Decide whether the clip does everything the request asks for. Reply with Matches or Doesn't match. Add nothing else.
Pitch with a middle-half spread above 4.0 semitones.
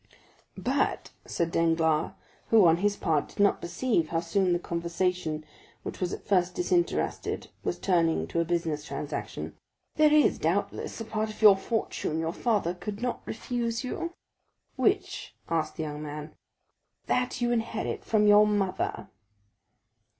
Matches